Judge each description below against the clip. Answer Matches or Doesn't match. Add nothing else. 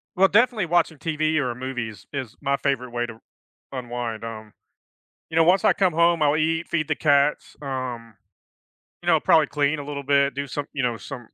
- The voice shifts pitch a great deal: Doesn't match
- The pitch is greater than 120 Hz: Matches